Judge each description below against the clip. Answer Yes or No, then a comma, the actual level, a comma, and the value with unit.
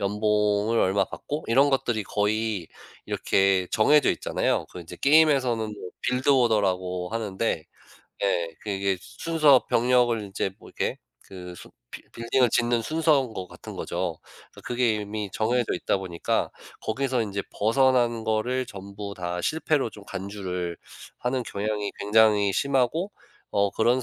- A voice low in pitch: Yes, low, 110 Hz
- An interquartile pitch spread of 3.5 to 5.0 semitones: Yes, average, 4.0 semitones